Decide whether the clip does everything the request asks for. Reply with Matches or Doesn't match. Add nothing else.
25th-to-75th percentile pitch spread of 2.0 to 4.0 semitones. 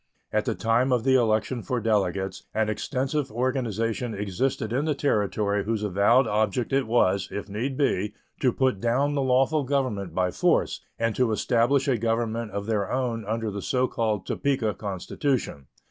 Matches